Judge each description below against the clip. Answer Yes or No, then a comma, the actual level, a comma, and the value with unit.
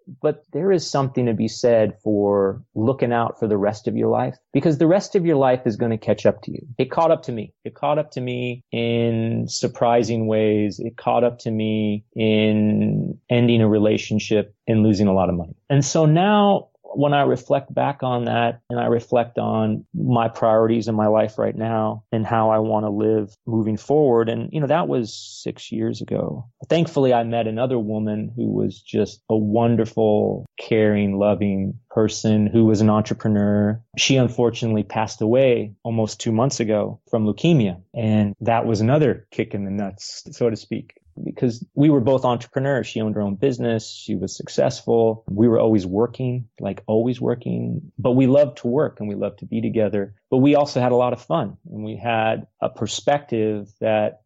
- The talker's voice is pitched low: Yes, low, 115 Hz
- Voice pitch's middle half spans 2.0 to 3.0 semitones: Yes, average, 2.7 semitones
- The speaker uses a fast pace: No, average, 195 wpm